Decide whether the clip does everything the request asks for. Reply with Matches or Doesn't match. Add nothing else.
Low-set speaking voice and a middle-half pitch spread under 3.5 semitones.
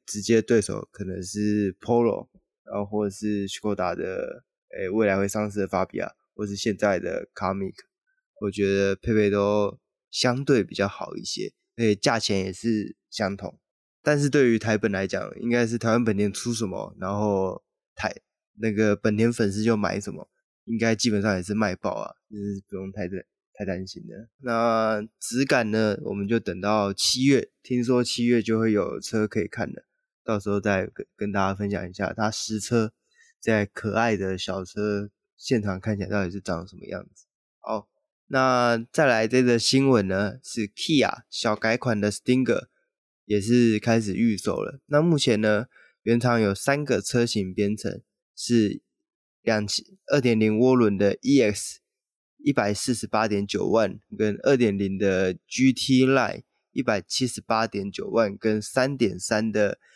Matches